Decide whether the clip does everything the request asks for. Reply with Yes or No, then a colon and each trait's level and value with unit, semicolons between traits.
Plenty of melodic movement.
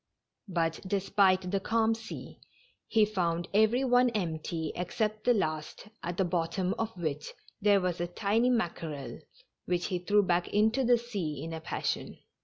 No: average, 4.3 semitones